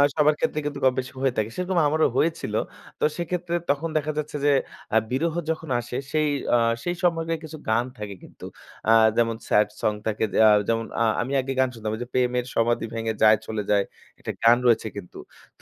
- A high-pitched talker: No, low, 125 Hz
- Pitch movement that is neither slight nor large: No, wide, 5.7 semitones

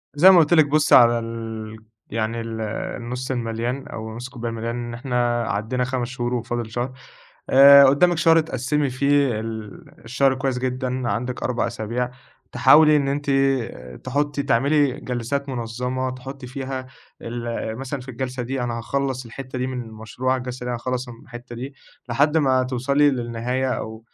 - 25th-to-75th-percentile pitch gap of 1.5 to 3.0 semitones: Yes, narrow, 2.4 semitones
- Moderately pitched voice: No, low, 125 Hz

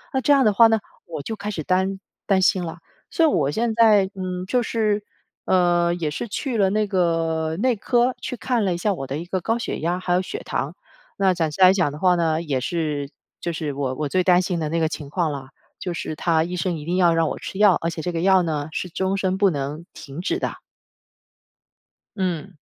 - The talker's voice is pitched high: No, medium, 180 Hz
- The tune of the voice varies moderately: Yes, average, 3.4 semitones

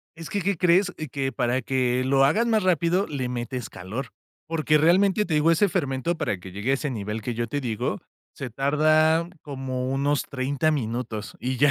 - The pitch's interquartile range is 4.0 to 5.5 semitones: Yes, average, 4.5 semitones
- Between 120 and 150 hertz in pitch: Yes, medium, 140 Hz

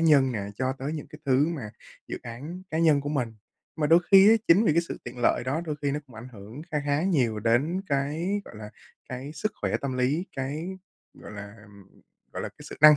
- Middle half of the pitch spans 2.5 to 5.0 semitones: Yes, average, 4.6 semitones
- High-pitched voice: No, medium, 140 Hz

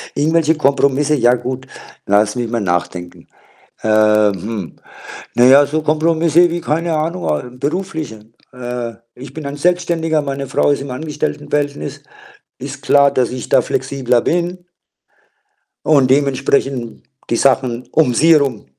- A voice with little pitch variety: No, average, 4.1 semitones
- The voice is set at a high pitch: No, medium, 140 Hz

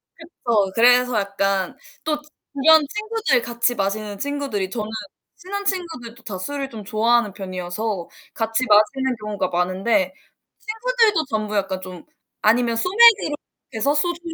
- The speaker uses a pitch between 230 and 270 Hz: Yes, high, 235 Hz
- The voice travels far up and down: Yes, wide, 6.9 semitones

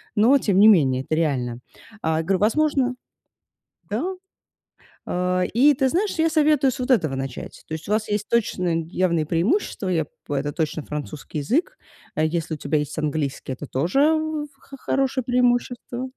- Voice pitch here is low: No, medium, 185 Hz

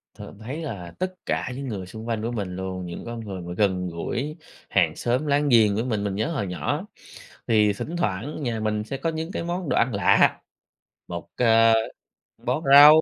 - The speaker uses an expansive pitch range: Yes, wide, 6.2 semitones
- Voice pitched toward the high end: No, low, 115 Hz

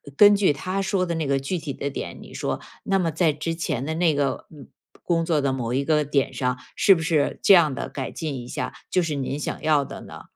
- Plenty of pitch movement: No, average, 3.6 semitones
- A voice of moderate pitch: Yes, medium, 155 Hz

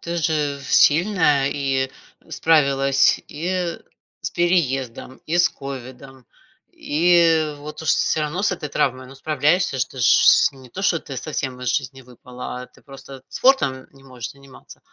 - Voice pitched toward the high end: No, medium, 140 Hz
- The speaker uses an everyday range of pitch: Yes, average, 3.6 semitones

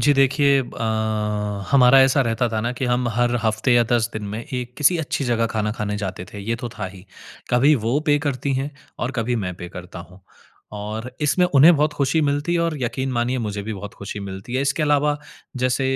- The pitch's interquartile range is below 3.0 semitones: No, average, 4.3 semitones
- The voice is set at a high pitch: No, low, 125 Hz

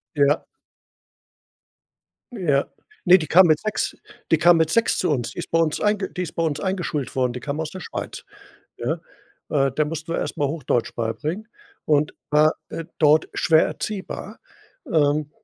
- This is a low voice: No, medium, 155 Hz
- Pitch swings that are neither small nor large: Yes, average, 3.1 semitones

